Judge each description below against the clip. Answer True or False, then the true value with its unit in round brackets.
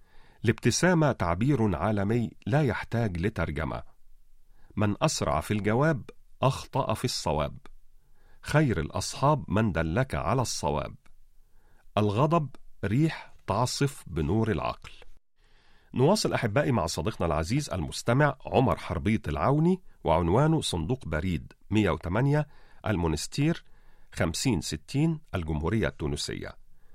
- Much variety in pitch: True (8.2 semitones)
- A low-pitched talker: True (110 Hz)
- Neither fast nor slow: True (90 wpm)